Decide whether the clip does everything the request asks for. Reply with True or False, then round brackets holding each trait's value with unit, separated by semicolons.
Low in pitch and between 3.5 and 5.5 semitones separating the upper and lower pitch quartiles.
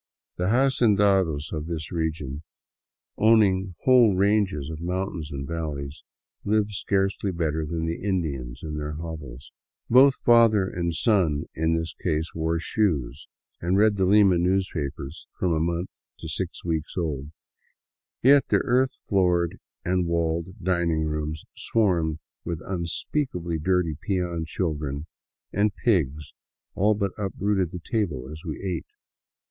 True (85 Hz; 3.9 semitones)